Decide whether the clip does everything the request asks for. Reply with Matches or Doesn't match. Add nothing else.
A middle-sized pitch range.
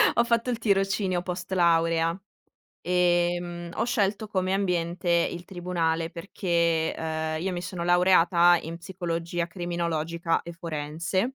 Doesn't match